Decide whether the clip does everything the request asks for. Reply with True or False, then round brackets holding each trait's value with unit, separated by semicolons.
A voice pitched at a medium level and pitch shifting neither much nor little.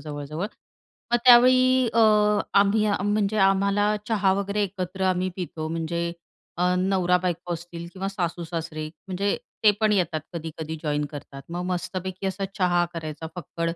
True (180 Hz; 3.1 semitones)